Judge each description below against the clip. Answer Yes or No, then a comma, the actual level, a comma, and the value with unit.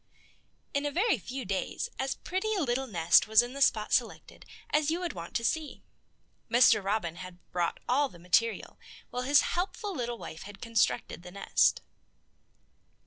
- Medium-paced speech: Yes, average, 170 wpm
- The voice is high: Yes, high, 240 Hz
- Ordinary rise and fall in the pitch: No, wide, 6.5 semitones